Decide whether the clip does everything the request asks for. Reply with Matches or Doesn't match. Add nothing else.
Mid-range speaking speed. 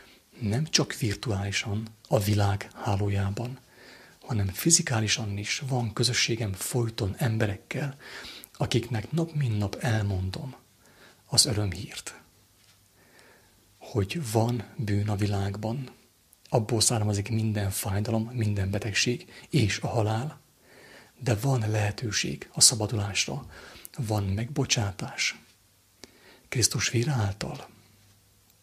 Doesn't match